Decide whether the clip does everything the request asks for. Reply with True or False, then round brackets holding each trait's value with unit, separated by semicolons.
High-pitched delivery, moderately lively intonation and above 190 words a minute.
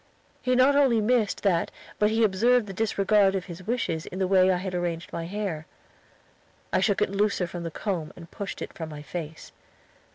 True (195 Hz; 3.7 semitones; 200 wpm)